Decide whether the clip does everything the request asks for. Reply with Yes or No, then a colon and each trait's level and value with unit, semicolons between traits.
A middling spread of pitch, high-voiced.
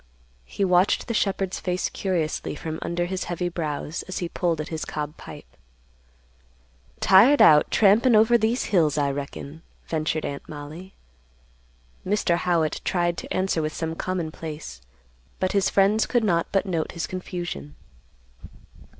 No: average, 3.6 semitones; medium, 175 Hz